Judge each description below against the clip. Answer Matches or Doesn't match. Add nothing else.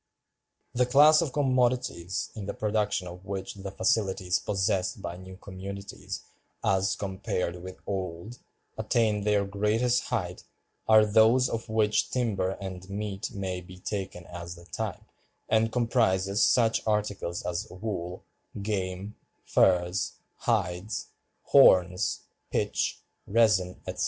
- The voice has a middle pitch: Doesn't match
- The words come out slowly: Matches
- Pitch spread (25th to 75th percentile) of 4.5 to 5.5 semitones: Doesn't match